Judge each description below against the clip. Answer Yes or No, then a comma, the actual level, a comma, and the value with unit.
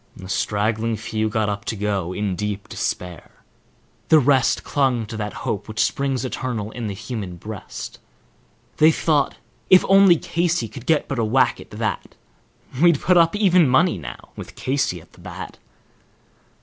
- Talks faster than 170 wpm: No, average, 165 wpm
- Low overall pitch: Yes, low, 115 Hz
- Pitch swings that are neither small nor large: No, wide, 6.0 semitones